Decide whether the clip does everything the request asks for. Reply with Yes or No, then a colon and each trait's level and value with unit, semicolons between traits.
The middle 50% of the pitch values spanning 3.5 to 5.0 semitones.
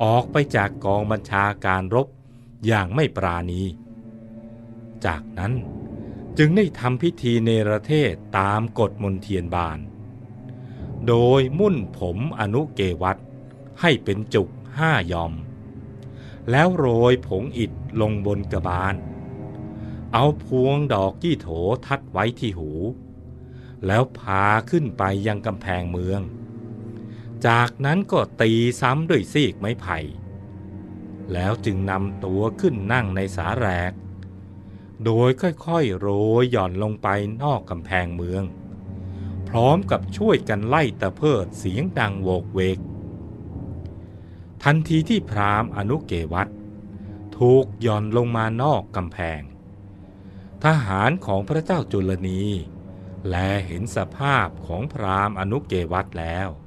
Yes: average, 4.5 semitones